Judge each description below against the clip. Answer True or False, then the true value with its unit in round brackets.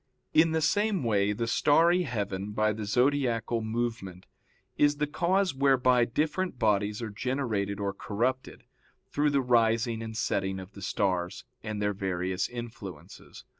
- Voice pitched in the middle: False (115 Hz)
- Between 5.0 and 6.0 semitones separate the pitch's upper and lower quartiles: True (5.3 semitones)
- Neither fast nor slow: True (145 wpm)